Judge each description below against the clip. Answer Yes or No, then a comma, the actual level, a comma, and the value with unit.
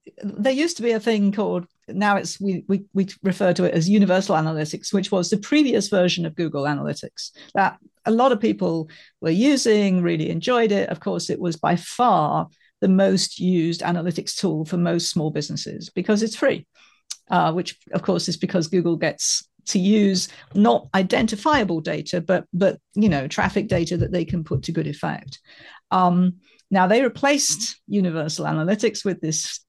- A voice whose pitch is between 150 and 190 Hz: Yes, medium, 185 Hz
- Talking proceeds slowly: No, average, 180 wpm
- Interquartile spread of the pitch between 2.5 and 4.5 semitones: Yes, average, 3.4 semitones